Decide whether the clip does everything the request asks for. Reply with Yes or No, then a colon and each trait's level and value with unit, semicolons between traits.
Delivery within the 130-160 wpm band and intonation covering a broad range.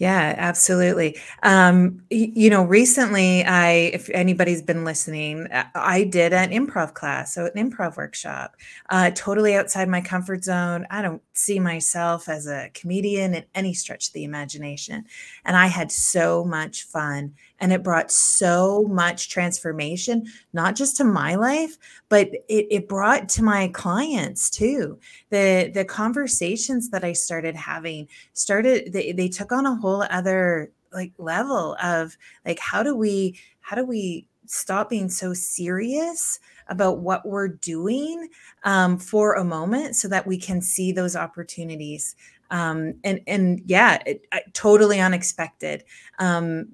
No: average, 150 wpm; average, 3.3 semitones